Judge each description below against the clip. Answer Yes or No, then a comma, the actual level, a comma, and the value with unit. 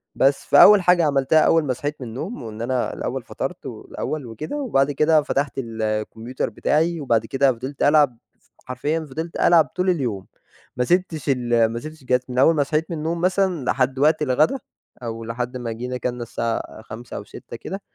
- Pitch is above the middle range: No, low, 135 Hz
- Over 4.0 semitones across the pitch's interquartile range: Yes, average, 4.7 semitones